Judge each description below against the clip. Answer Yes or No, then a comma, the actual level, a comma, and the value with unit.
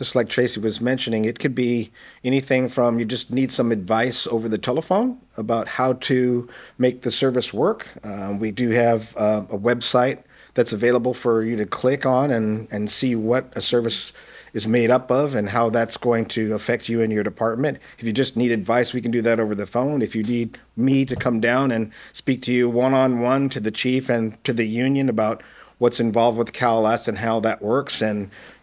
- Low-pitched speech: Yes, low, 120 Hz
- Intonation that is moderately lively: No, narrow, 2.1 semitones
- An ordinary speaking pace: No, fast, 215 wpm